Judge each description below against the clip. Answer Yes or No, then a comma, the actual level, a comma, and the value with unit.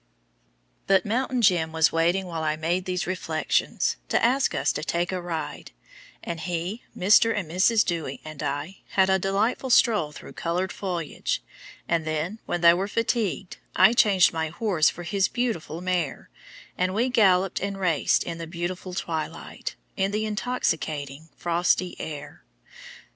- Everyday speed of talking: Yes, average, 155 wpm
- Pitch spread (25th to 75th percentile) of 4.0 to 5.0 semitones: No, average, 3.4 semitones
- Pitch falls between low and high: Yes, medium, 180 Hz